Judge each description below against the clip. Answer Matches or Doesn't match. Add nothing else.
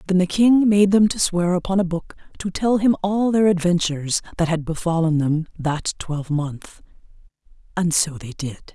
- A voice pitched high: Doesn't match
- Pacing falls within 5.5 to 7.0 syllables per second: Doesn't match